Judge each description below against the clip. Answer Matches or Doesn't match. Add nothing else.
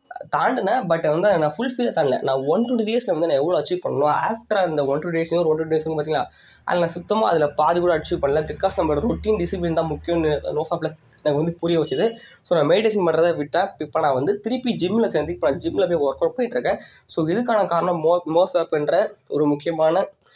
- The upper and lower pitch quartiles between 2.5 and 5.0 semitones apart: Doesn't match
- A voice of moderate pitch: Matches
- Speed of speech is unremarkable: Doesn't match